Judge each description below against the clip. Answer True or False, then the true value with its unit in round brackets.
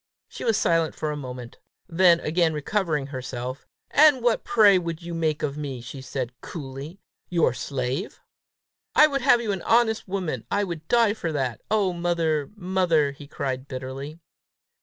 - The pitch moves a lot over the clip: True (5.7 semitones)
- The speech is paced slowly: False (165 wpm)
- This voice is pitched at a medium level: True (160 Hz)